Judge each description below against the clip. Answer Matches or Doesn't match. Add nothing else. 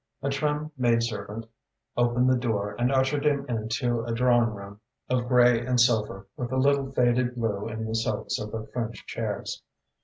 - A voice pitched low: Matches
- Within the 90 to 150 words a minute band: Doesn't match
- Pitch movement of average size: Doesn't match